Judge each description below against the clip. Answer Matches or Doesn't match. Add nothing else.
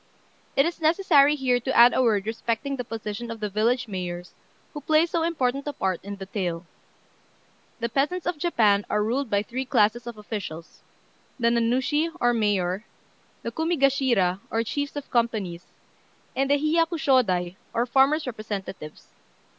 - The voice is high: Matches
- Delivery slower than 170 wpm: Matches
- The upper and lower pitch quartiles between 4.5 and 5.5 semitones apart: Matches